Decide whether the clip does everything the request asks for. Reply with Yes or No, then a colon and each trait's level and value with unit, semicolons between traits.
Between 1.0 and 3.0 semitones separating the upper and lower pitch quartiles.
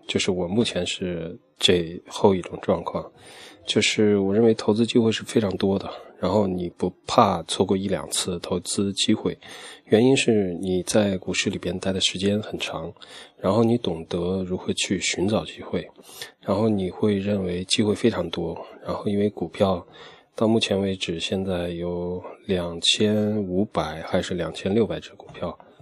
Yes: average, 2.7 semitones